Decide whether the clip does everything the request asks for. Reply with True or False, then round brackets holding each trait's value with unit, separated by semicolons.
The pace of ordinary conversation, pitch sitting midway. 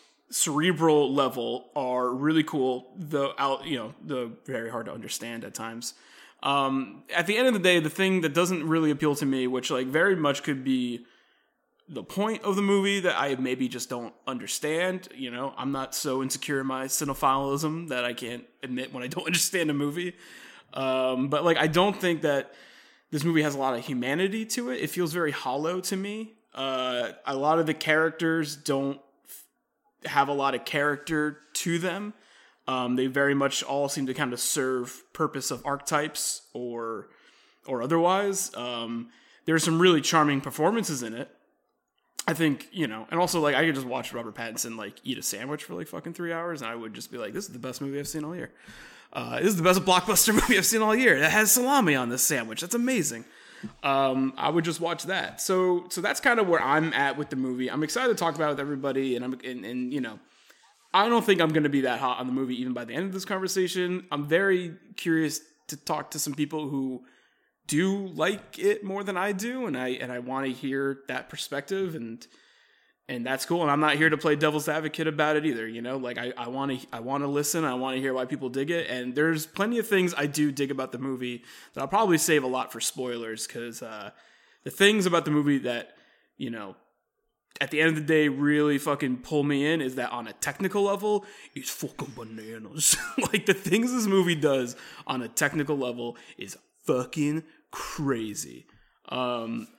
False (210 wpm; 150 Hz)